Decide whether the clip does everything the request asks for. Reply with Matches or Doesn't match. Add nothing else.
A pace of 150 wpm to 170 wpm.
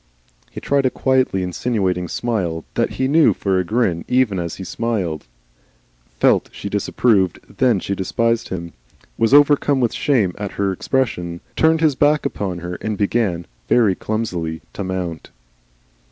Matches